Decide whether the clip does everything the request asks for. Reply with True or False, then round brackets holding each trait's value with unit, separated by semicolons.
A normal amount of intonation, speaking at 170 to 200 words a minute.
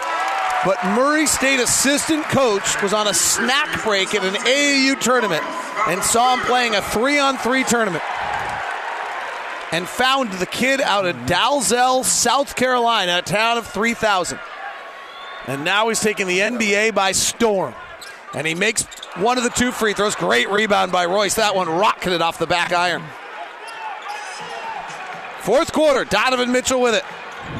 False (4.6 semitones; 150 wpm)